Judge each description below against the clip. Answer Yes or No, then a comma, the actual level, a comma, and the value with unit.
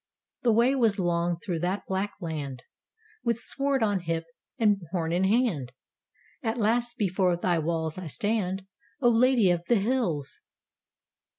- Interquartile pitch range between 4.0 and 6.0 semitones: Yes, average, 5.3 semitones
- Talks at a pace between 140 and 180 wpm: Yes, average, 150 wpm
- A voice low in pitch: No, high, 190 Hz